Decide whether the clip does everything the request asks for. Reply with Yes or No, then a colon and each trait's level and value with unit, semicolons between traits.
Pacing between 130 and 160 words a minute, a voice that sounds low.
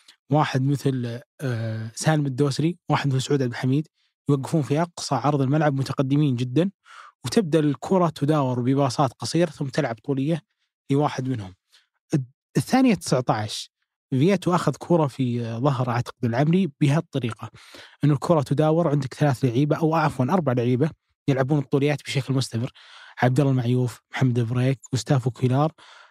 No: fast, 135 wpm; medium, 145 Hz